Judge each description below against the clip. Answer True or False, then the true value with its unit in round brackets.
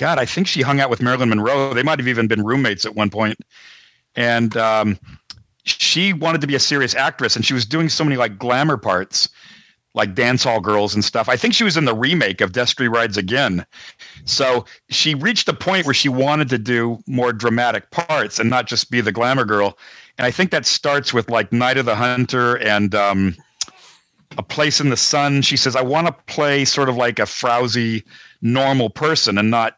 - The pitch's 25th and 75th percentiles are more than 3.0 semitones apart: True (3.7 semitones)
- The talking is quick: True (210 wpm)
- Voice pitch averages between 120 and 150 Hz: True (125 Hz)